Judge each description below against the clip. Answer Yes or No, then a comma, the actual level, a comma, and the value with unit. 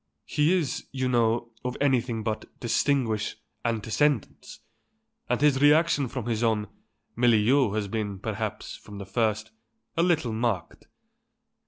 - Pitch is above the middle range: No, low, 120 Hz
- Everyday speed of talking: No, slow, 130 wpm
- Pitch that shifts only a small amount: No, average, 3.9 semitones